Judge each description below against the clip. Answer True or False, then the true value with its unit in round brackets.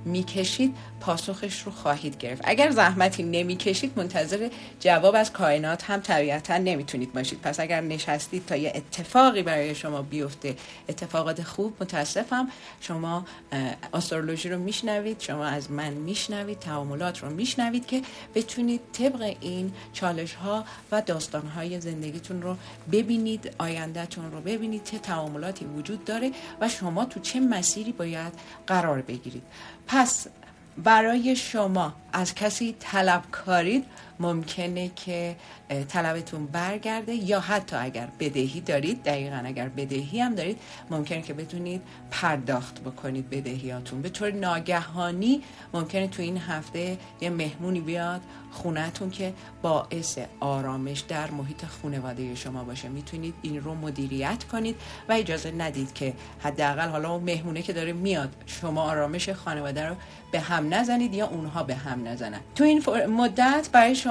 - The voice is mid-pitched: True (170 Hz)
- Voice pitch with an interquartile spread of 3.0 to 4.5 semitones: False (5.3 semitones)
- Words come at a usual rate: True (135 wpm)